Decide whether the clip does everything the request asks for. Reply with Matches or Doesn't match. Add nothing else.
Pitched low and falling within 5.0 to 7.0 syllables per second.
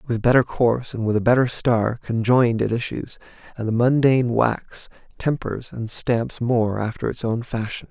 Doesn't match